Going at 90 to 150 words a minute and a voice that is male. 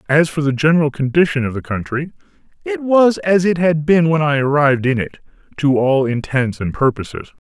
No: average, 195 wpm; male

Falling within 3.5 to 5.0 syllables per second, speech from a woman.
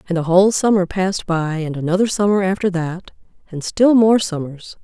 No: 5.4 syllables/s; female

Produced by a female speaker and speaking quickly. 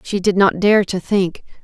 Yes: female; fast, 220 wpm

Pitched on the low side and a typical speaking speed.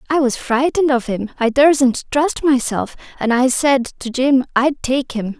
No: very high, 260 Hz; average, 190 wpm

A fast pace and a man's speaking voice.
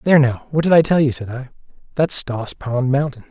Yes: fast, 235 wpm; male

